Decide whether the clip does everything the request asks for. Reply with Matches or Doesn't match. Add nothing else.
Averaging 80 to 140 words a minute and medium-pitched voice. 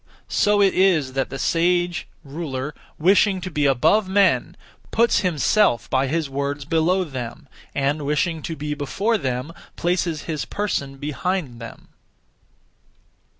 Matches